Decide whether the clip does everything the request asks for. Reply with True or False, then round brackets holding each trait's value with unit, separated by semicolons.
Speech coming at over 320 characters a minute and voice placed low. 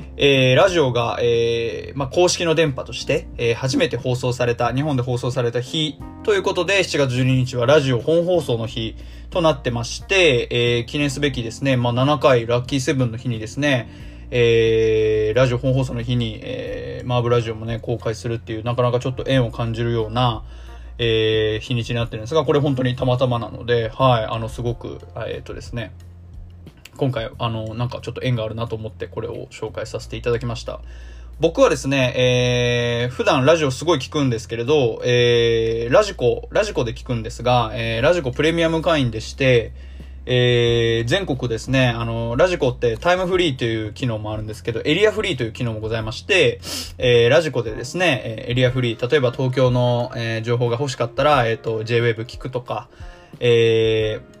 True (385 characters per minute; 120 Hz)